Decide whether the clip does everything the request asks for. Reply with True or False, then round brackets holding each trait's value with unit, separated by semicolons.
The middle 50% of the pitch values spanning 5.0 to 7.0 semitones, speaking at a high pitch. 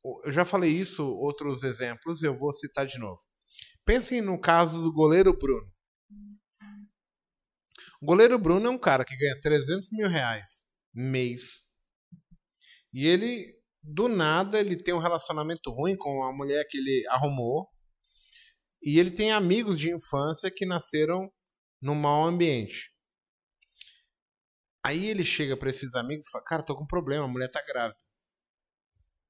False (5.3 semitones; 160 Hz)